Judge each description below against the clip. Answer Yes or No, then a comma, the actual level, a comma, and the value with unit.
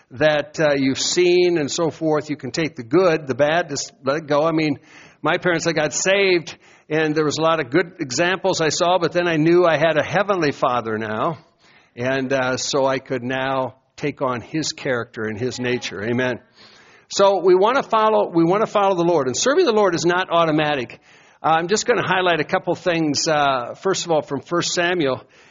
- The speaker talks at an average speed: No, fast, 215 wpm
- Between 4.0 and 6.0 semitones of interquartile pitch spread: Yes, average, 4.7 semitones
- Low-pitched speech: No, medium, 155 Hz